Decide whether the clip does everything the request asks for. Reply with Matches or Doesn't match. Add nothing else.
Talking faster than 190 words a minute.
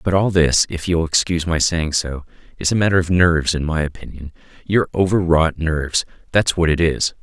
Matches